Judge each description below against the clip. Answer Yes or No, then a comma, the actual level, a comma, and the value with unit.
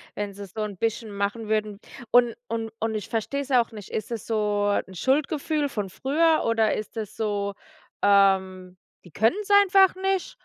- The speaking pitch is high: Yes, high, 220 Hz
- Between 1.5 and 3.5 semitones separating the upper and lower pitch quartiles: No, average, 4.3 semitones